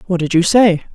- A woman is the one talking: Yes, female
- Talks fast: Yes, fast, 255 wpm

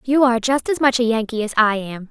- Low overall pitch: No, high, 235 Hz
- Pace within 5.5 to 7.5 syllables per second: Yes, 6.1 syllables/s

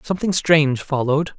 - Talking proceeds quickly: No, slow, 130 wpm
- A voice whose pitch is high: No, medium, 150 Hz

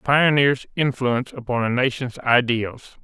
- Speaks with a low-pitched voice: Yes, low, 125 Hz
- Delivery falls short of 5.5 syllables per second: Yes, 4.5 syllables/s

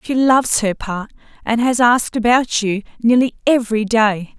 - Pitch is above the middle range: Yes, high, 230 Hz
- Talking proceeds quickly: No, average, 165 wpm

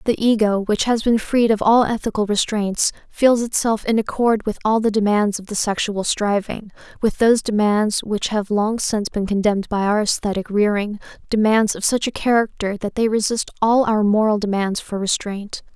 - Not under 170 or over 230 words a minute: Yes, average, 185 wpm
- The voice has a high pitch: Yes, high, 215 Hz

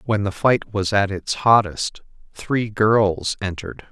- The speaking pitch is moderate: No, low, 100 Hz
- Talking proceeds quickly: No, average, 155 wpm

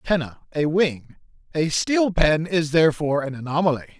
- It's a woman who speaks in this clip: No, male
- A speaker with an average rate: Yes, average, 150 wpm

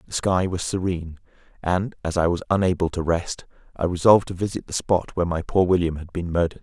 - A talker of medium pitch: No, very low, 90 Hz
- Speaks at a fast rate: Yes, fast, 215 wpm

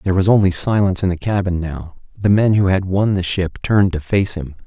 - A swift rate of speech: Yes, fast, 245 wpm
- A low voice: Yes, very low, 95 Hz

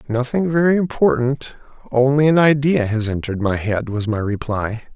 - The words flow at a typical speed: Yes, average, 155 wpm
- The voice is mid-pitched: No, low, 125 Hz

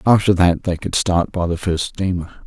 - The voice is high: No, very low, 90 Hz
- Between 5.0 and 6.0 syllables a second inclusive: Yes, 5.1 syllables/s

